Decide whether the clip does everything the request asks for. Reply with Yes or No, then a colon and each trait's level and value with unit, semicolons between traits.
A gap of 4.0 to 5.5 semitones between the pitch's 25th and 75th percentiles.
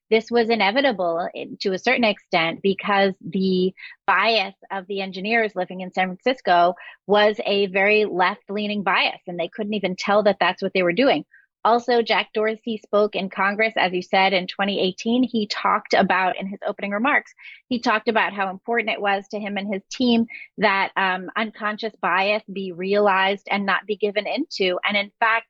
No: average, 2.7 semitones